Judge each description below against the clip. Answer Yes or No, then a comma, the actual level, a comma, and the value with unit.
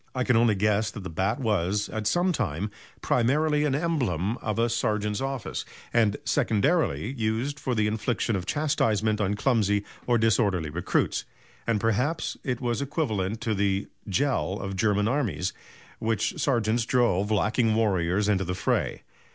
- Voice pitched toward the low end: Yes, low, 110 Hz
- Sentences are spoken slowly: No, average, 160 wpm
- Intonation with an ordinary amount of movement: Yes, average, 3.5 semitones